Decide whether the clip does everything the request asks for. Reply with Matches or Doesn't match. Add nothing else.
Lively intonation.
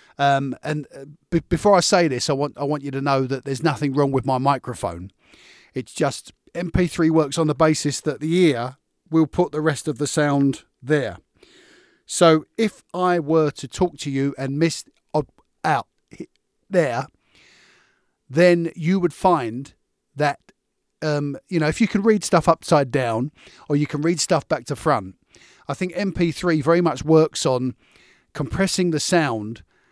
Doesn't match